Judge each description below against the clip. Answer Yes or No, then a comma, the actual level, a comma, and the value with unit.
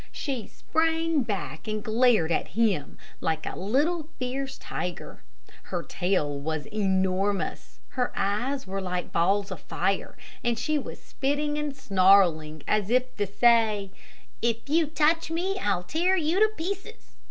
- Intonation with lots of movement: Yes, wide, 7.7 semitones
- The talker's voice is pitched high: Yes, high, 225 Hz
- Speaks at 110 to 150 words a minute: Yes, average, 145 wpm